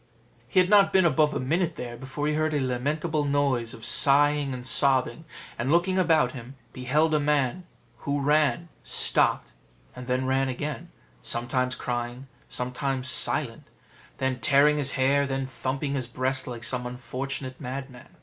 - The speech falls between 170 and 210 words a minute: No, average, 155 wpm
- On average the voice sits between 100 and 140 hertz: Yes, low, 135 Hz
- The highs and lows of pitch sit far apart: No, average, 2.8 semitones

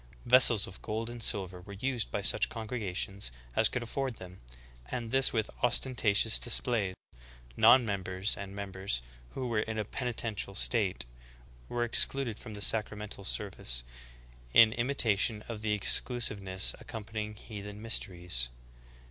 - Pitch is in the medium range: No, low, 105 Hz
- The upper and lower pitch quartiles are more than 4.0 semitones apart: No, average, 3.2 semitones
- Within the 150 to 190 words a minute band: No, average, 140 wpm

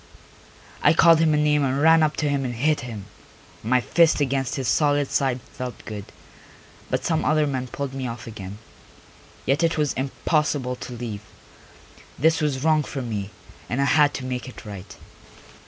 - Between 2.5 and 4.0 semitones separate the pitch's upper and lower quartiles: Yes, average, 3.6 semitones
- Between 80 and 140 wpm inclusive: No, average, 180 wpm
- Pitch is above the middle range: No, low, 135 Hz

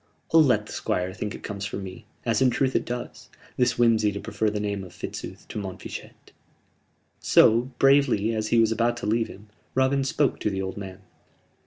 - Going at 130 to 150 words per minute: No, average, 200 wpm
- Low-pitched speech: Yes, low, 110 Hz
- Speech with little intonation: No, average, 3.3 semitones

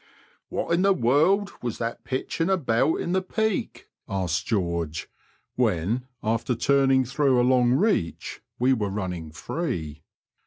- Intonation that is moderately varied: No, wide, 8.6 semitones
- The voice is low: Yes, low, 125 Hz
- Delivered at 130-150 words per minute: Yes, average, 145 wpm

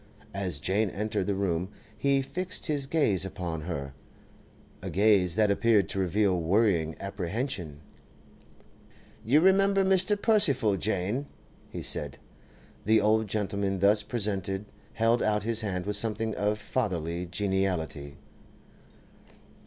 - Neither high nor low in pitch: No, low, 100 Hz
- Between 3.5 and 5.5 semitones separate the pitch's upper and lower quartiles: Yes, average, 3.8 semitones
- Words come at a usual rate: No, slow, 120 wpm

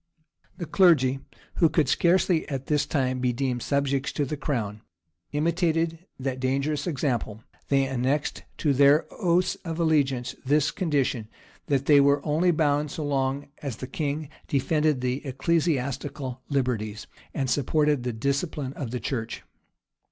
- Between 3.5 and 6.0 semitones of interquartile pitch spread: No, average, 3.0 semitones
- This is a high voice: No, medium, 140 Hz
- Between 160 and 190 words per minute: No, average, 145 wpm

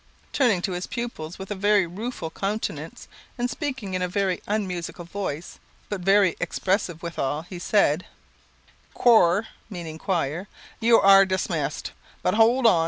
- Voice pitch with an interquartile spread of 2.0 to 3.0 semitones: No, average, 3.5 semitones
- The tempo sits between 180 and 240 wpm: No, average, 145 wpm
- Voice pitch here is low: No, high, 190 Hz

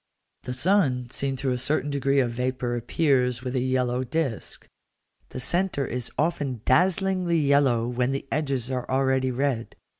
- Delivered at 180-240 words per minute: No, average, 155 wpm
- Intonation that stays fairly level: Yes, narrow, 2.3 semitones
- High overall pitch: No, low, 130 Hz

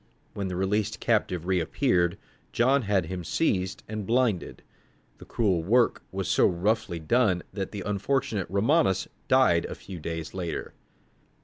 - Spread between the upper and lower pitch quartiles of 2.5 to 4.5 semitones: Yes, average, 4.0 semitones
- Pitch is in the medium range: No, very low, 95 Hz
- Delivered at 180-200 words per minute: No, average, 140 wpm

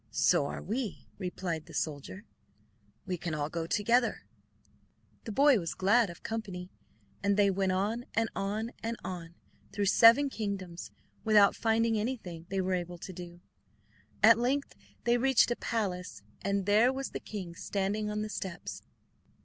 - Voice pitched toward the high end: Yes, high, 200 Hz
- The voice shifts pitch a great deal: No, average, 4.0 semitones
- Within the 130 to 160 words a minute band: Yes, average, 155 wpm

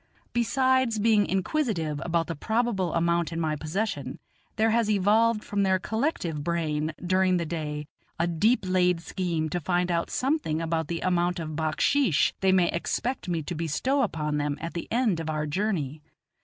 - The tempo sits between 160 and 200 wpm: Yes, average, 170 wpm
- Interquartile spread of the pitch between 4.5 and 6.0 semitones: Yes, average, 5.1 semitones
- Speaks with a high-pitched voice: No, medium, 175 Hz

